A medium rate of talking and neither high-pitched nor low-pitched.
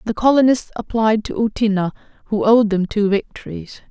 No: average, 155 wpm; high, 215 Hz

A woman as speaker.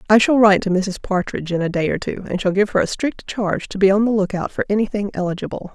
Yes: female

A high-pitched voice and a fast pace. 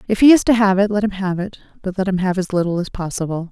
Yes: high, 195 Hz; fast, 310 wpm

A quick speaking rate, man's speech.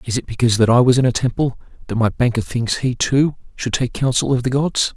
Yes: fast, 255 wpm; male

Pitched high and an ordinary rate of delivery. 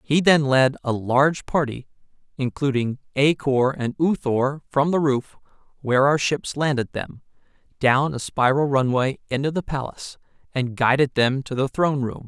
No: low, 135 Hz; average, 165 wpm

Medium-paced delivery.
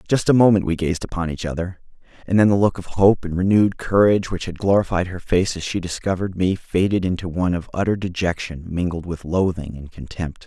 No: fast, 210 wpm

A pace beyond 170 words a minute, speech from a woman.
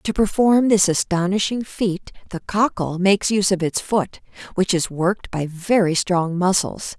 No: average, 165 wpm; female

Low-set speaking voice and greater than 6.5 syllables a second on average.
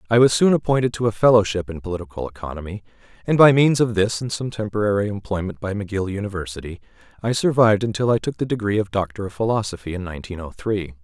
Yes: low, 105 Hz; 6.8 syllables/s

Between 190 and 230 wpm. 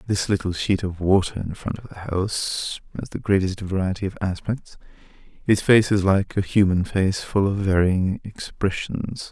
No: average, 175 wpm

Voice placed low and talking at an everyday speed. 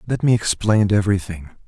Yes: low, 100 Hz; average, 145 wpm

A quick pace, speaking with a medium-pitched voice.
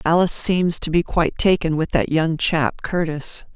No: average, 185 wpm; medium, 160 Hz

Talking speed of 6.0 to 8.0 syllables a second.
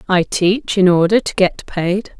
No: 4.0 syllables/s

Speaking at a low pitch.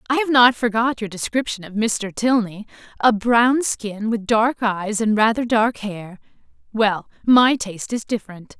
No: high, 220 Hz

